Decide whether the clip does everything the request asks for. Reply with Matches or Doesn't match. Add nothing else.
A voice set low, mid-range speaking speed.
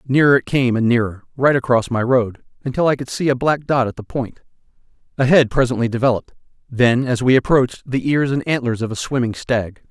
Doesn't match